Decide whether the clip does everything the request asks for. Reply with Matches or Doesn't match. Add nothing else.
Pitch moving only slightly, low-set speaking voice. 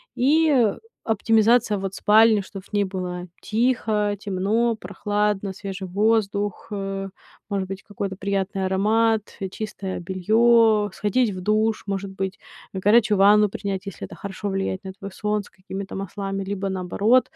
Doesn't match